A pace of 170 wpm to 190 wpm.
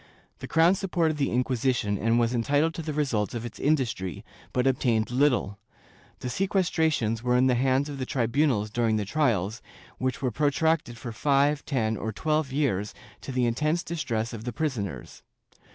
Yes: average, 175 wpm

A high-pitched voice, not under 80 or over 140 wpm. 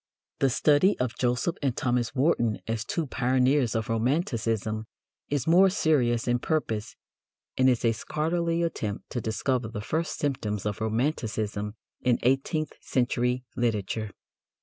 No: low, 125 Hz; slow, 135 wpm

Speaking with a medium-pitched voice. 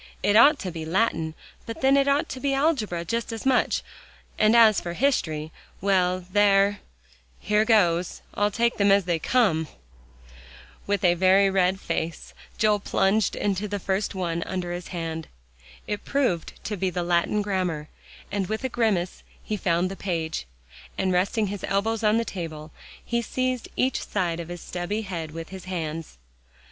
No: high, 195 Hz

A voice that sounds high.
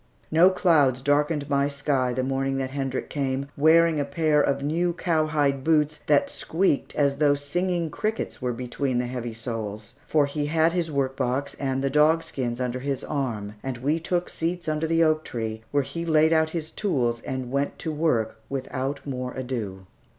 No: medium, 140 Hz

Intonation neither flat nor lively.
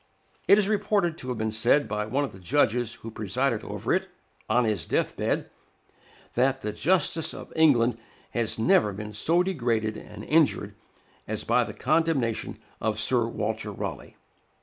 No: wide, 6.5 semitones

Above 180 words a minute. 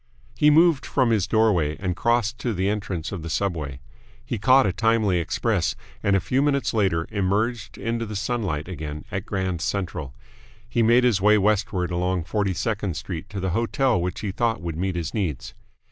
Yes: average, 190 wpm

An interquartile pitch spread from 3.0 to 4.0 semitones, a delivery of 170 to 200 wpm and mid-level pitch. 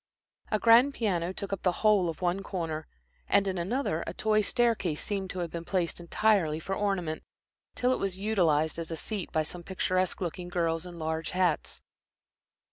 Yes: average, 3.3 semitones; average, 185 wpm; medium, 180 Hz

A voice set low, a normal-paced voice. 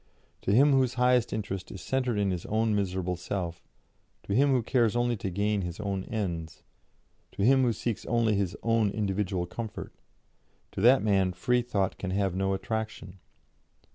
Yes: low, 105 Hz; average, 170 wpm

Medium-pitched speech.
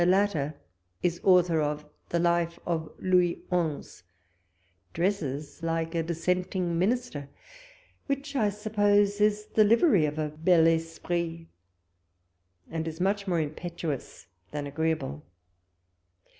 Yes: medium, 170 Hz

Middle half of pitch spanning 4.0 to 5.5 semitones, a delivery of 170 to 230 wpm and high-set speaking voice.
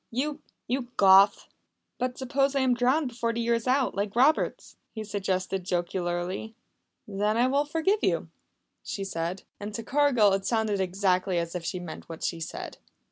Yes: average, 5.2 semitones; average, 175 wpm; high, 215 Hz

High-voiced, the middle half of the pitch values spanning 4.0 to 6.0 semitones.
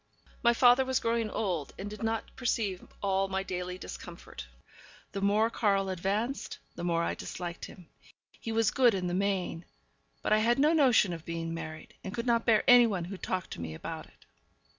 Yes: high, 200 Hz; average, 4.3 semitones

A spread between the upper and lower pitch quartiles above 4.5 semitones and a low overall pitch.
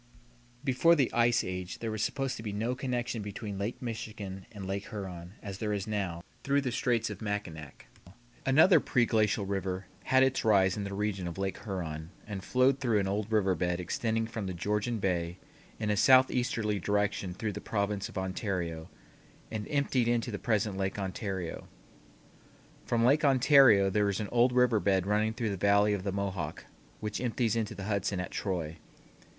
No: average, 3.3 semitones; low, 105 Hz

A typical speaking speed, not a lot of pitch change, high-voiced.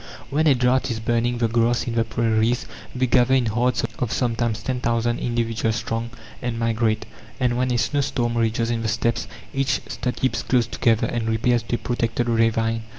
No: average, 190 wpm; narrow, 1.4 semitones; low, 120 Hz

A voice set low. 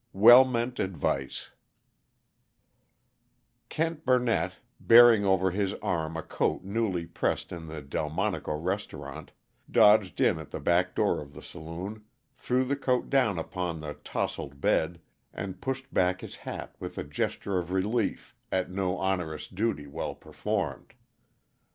Yes: very low, 95 Hz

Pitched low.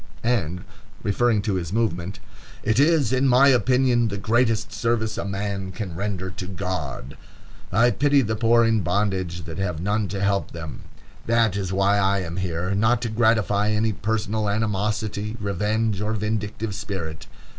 Yes: low, 105 Hz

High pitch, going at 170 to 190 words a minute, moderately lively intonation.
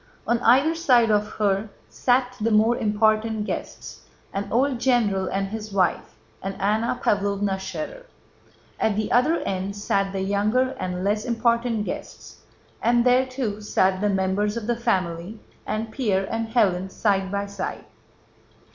No: high, 210 Hz; average, 145 wpm; average, 3.2 semitones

